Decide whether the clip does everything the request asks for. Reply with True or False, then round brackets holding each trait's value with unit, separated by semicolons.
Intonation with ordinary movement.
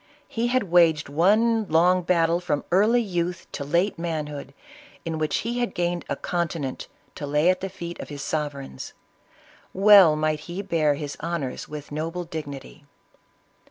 True (3.4 semitones)